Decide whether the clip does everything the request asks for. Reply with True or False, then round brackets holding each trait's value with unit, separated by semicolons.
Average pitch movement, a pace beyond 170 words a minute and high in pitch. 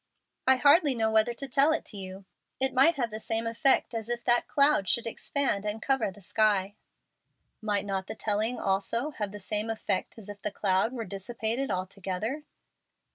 True (3.8 semitones; 185 wpm; 220 Hz)